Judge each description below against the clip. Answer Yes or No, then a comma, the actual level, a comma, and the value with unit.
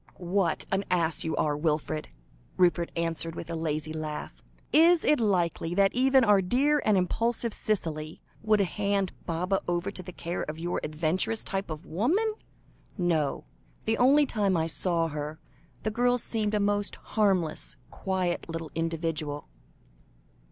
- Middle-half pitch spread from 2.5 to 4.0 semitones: No, average, 4.4 semitones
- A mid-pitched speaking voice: Yes, medium, 180 Hz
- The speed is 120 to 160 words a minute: Yes, average, 150 wpm